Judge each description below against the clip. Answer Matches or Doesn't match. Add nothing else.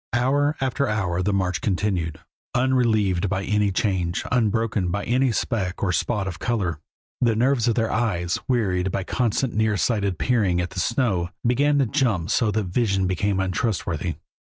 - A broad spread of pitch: Doesn't match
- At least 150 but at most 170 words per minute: Matches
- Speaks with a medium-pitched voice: Doesn't match